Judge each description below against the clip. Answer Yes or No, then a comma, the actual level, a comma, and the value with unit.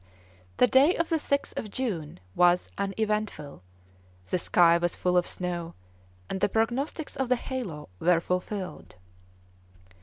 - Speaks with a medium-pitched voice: No, high, 195 Hz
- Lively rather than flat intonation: Yes, wide, 6.2 semitones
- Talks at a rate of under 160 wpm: Yes, average, 140 wpm